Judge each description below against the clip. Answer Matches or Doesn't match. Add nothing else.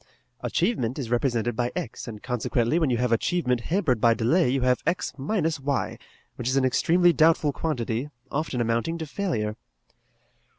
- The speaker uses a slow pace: Doesn't match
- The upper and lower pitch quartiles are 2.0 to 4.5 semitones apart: Doesn't match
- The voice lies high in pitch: Doesn't match